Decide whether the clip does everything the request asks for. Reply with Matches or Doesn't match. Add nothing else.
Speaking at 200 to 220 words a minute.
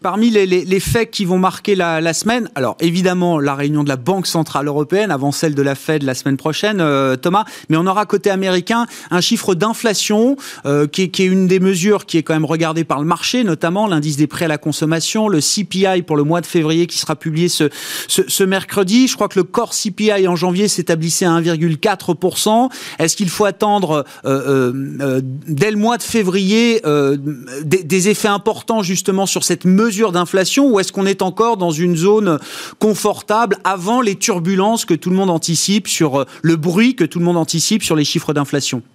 Matches